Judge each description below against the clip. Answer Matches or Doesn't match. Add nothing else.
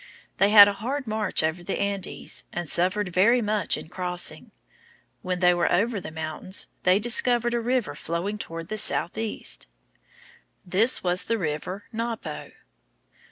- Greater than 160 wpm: Doesn't match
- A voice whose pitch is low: Doesn't match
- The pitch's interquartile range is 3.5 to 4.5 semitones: Matches